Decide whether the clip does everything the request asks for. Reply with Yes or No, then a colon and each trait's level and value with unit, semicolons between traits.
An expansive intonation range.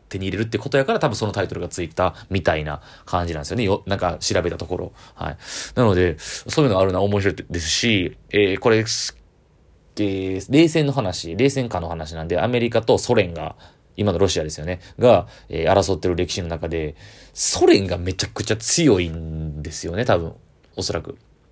No: average, 4.6 semitones